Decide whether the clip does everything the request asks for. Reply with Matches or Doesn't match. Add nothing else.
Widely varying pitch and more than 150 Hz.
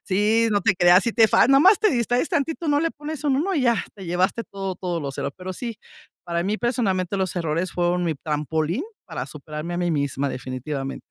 Matches